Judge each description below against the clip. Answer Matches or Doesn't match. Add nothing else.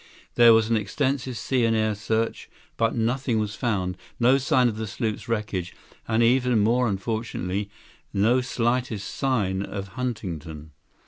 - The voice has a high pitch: Doesn't match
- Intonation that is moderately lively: Matches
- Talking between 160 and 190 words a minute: Doesn't match